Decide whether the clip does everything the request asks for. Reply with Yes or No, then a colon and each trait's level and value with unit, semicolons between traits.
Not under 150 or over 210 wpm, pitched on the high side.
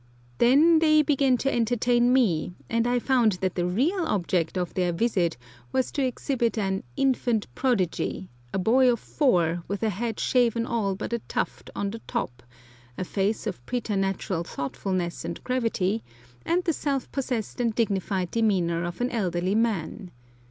Yes: average, 160 wpm; high, 220 Hz